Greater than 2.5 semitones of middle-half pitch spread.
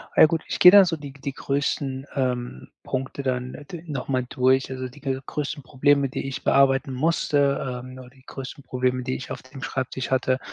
No: narrow, 1.7 semitones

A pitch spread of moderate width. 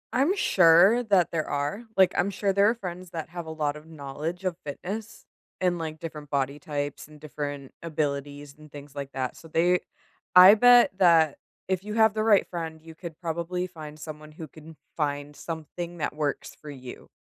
Yes: average, 3.6 semitones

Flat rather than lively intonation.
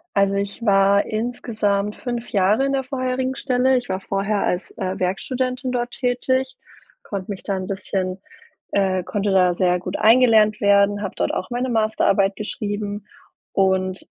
No: average, 4.1 semitones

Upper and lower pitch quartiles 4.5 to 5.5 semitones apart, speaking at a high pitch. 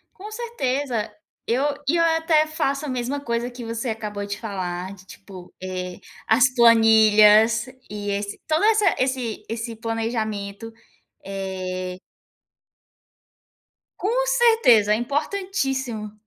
Yes: average, 5.2 semitones; high, 230 Hz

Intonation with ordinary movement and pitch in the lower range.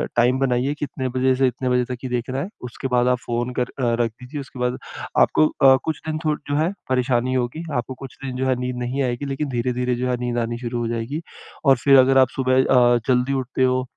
No: narrow, 1.6 semitones; low, 125 Hz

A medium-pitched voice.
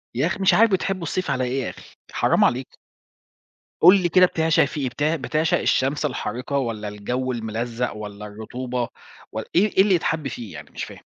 No: low, 130 Hz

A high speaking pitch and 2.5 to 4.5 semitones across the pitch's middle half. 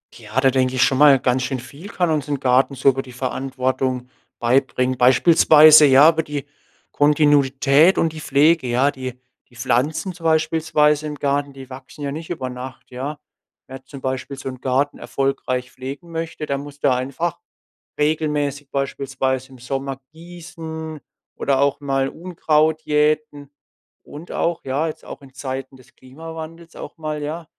No: medium, 140 Hz; average, 2.9 semitones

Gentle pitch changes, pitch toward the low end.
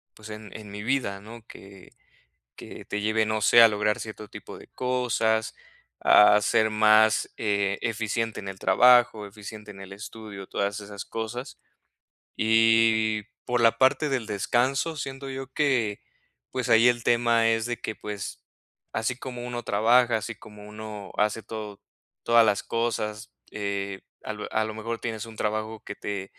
Yes: narrow, 2.0 semitones; low, 110 Hz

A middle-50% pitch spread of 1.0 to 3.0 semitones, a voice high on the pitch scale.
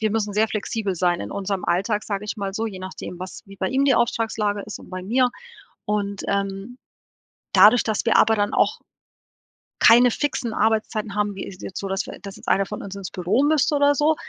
Yes: narrow, 2.5 semitones; high, 210 Hz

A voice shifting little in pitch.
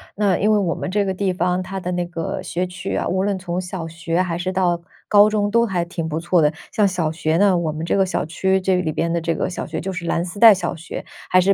Yes: narrow, 2.1 semitones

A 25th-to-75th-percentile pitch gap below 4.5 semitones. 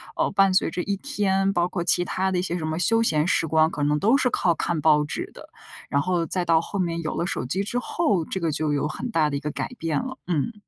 Yes: average, 3.7 semitones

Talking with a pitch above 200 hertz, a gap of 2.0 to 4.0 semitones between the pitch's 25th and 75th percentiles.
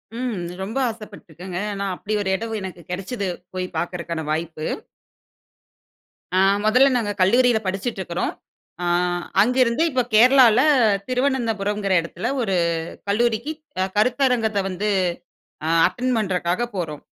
No: high, 210 Hz; average, 4.7 semitones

